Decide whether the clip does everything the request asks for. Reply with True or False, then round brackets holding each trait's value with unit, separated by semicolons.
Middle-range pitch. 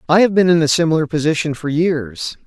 True (160 Hz)